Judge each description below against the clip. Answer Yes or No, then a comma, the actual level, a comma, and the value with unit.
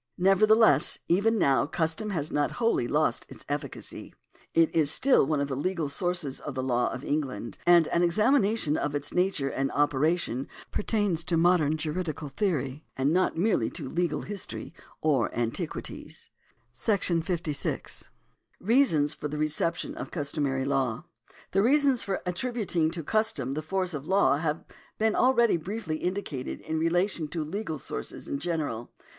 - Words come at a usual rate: Yes, average, 155 wpm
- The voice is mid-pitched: Yes, medium, 160 Hz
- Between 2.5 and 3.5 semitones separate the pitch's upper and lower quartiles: No, average, 5.0 semitones